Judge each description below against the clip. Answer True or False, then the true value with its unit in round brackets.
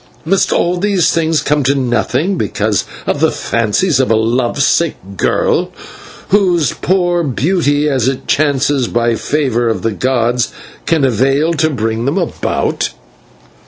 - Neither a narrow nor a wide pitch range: False (5.7 semitones)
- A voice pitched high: False (140 Hz)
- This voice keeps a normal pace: True (145 wpm)